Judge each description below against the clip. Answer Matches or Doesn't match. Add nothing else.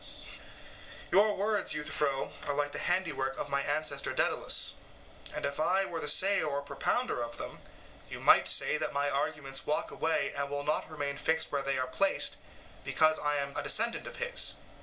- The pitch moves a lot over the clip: Doesn't match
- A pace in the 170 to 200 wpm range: Matches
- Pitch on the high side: Doesn't match